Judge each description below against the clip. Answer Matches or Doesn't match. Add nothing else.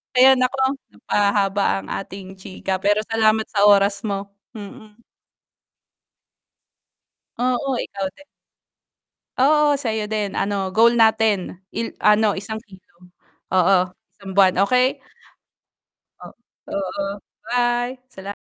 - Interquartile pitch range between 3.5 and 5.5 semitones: Doesn't match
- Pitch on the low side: Doesn't match